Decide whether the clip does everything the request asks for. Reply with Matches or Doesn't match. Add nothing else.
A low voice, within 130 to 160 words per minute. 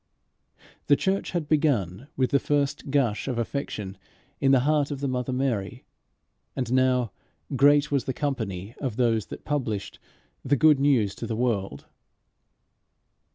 Matches